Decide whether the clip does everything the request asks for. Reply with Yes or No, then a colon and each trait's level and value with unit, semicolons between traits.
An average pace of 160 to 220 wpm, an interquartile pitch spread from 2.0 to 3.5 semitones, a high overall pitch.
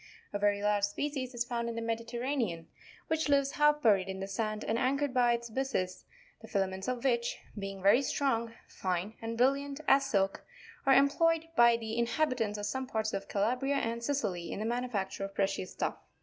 No: average, 190 wpm; average, 4.7 semitones; high, 235 Hz